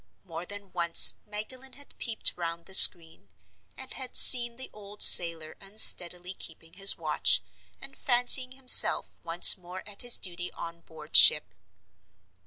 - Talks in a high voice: Yes, high, 195 Hz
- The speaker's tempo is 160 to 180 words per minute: No, average, 145 wpm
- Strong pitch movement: Yes, wide, 6.1 semitones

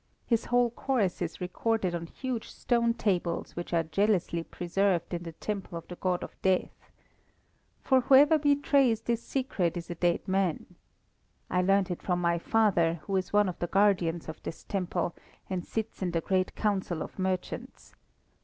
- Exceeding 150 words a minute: Yes, average, 170 wpm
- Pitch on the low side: No, medium, 185 Hz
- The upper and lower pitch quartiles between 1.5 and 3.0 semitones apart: No, average, 4.3 semitones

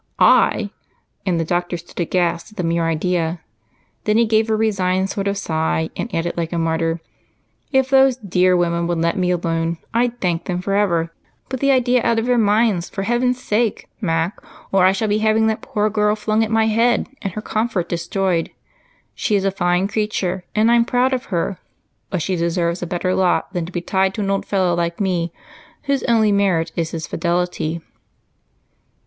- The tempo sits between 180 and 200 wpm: Yes, average, 195 wpm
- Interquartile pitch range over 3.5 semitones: Yes, average, 4.2 semitones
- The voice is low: No, high, 190 Hz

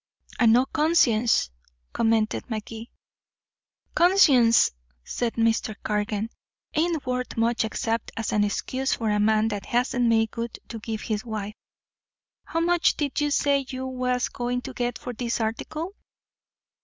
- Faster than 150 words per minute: No, average, 145 wpm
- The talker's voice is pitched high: Yes, high, 235 Hz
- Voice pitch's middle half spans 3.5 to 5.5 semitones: No, average, 2.7 semitones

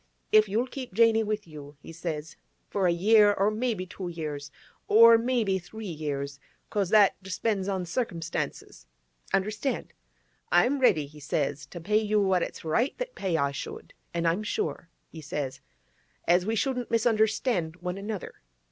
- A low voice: No, high, 190 Hz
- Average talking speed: Yes, average, 150 wpm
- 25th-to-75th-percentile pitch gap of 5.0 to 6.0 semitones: Yes, wide, 5.4 semitones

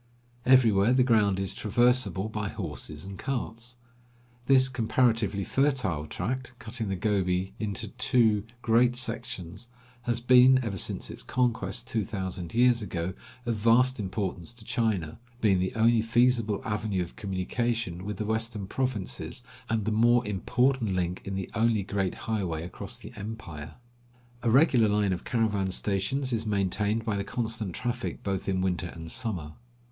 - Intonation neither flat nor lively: Yes, average, 3.8 semitones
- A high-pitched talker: No, low, 110 Hz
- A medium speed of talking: Yes, average, 150 wpm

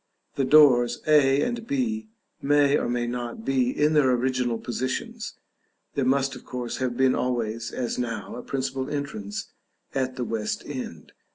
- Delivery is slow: No, average, 160 wpm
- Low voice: Yes, low, 130 Hz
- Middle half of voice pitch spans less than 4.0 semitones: Yes, average, 2.7 semitones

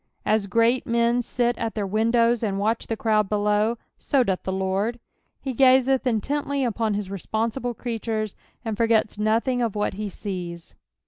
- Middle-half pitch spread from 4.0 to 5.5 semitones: No, narrow, 2.5 semitones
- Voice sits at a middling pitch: No, high, 225 Hz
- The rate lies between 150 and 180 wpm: Yes, average, 165 wpm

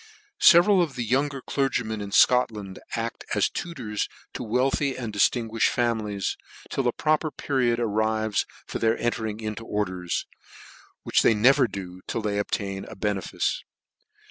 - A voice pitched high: No, low, 115 Hz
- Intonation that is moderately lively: Yes, average, 3.7 semitones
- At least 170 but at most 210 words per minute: No, average, 145 wpm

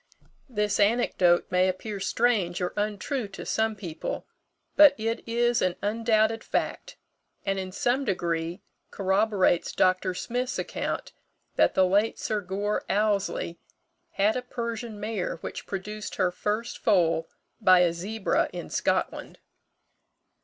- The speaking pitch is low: No, high, 205 Hz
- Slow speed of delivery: Yes, slow, 130 wpm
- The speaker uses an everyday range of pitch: Yes, average, 3.2 semitones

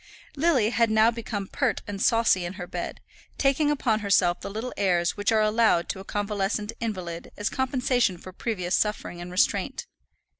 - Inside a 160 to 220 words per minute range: Yes, average, 175 wpm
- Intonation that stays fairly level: No, average, 3.7 semitones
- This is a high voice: Yes, high, 210 Hz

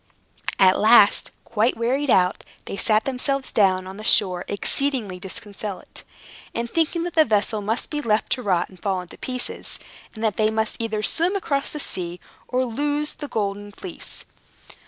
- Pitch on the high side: Yes, high, 220 Hz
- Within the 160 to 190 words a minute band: Yes, average, 170 wpm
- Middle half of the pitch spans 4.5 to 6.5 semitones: Yes, average, 5.1 semitones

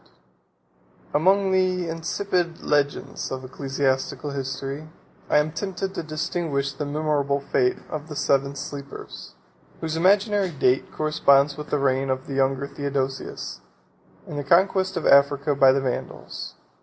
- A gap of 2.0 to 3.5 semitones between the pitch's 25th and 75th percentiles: Yes, average, 3.2 semitones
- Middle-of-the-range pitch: Yes, medium, 145 Hz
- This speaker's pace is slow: No, average, 145 wpm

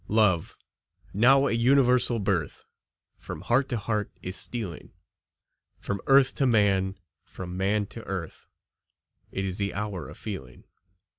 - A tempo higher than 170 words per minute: No, slow, 135 wpm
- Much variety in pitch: No, average, 3.9 semitones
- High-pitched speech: No, low, 105 Hz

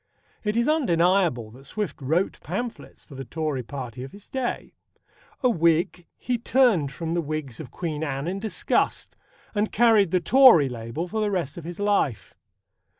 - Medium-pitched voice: Yes, medium, 170 Hz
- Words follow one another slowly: No, average, 170 wpm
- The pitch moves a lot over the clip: Yes, wide, 6.6 semitones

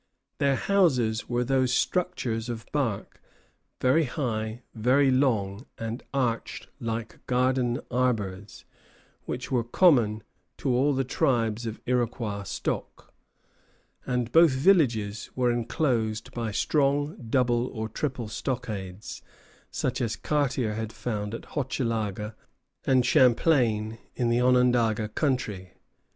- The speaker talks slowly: Yes, slow, 115 wpm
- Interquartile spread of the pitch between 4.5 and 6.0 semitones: No, average, 3.0 semitones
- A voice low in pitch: Yes, low, 120 Hz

